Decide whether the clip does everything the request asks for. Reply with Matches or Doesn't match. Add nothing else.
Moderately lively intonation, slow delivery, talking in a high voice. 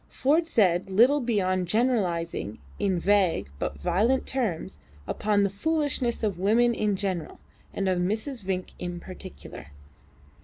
Matches